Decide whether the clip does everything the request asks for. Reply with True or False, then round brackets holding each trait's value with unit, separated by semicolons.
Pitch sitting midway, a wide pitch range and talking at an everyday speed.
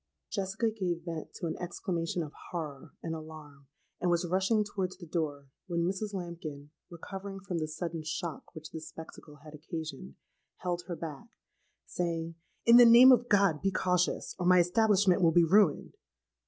False (175 Hz; 3.3 semitones; 170 wpm)